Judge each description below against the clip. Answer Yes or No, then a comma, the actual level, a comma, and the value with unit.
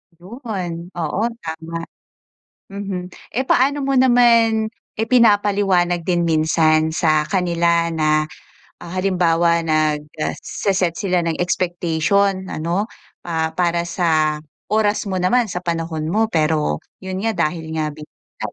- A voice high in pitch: No, medium, 175 Hz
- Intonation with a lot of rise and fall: No, average, 3.7 semitones